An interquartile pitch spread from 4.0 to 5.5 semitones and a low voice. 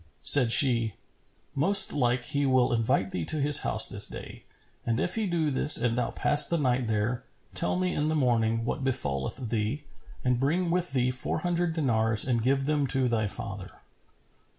Yes: average, 4.4 semitones; low, 130 Hz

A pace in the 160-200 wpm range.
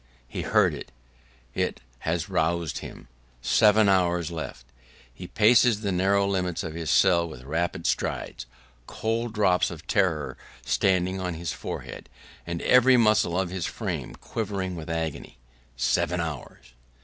No: average, 140 wpm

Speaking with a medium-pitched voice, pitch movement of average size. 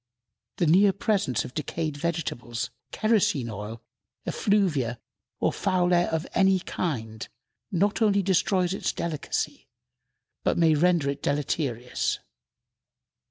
No: medium, 165 Hz; wide, 6.2 semitones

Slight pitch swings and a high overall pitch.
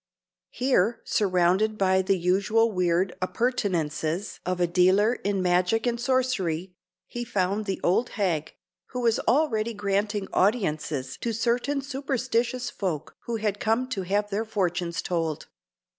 No: average, 4.4 semitones; high, 205 Hz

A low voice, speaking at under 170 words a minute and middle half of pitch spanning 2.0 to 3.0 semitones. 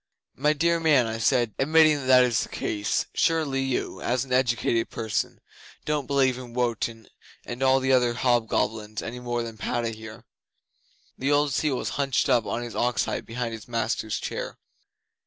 No: low, 125 Hz; average, 175 wpm; average, 2.7 semitones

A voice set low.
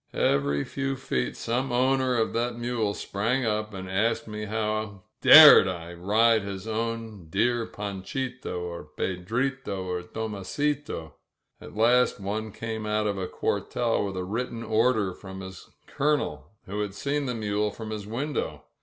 Yes: low, 110 Hz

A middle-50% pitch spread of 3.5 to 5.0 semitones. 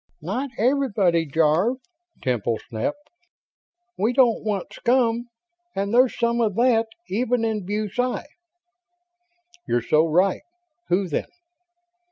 No: wide, 5.5 semitones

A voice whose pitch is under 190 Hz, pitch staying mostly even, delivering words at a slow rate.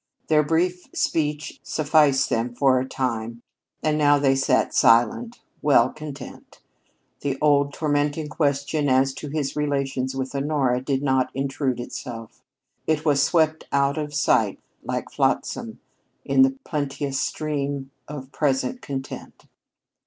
Yes: medium, 140 Hz; narrow, 2.2 semitones; slow, 130 wpm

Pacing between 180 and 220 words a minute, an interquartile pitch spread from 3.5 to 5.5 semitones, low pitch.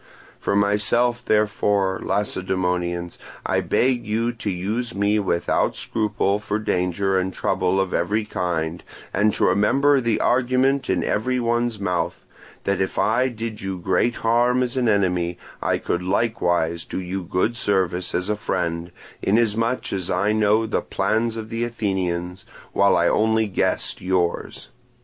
No: average, 150 wpm; average, 4.0 semitones; low, 100 Hz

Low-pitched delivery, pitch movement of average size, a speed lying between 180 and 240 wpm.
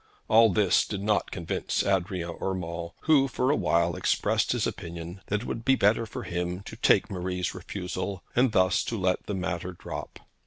Yes: very low, 95 Hz; average, 3.1 semitones; average, 185 wpm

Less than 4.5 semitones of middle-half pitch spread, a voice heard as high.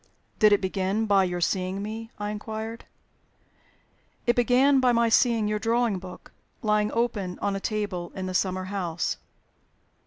Yes: average, 3.2 semitones; high, 210 Hz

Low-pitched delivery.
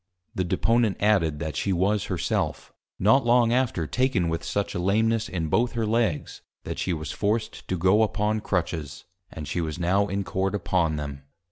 Yes: very low, 95 Hz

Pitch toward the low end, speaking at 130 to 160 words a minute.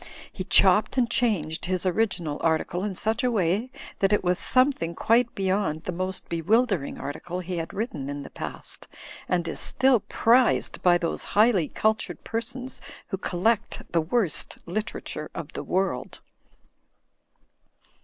No: high, 190 Hz; average, 150 wpm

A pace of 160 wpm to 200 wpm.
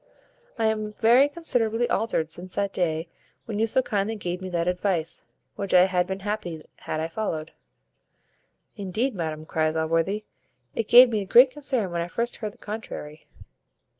Yes: average, 165 wpm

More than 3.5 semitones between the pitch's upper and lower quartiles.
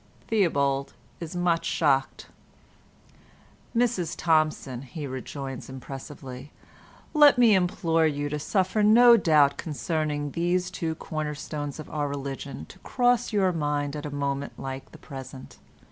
Yes: average, 4.2 semitones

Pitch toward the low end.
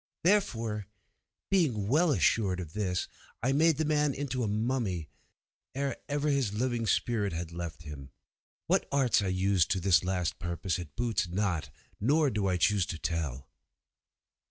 Yes: low, 105 Hz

